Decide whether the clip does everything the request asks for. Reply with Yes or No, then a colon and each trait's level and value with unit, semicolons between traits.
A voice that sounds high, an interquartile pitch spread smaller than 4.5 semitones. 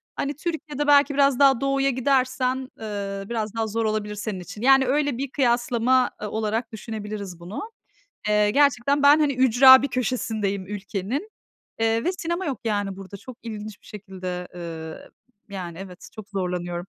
No: high, 225 Hz; average, 5.1 semitones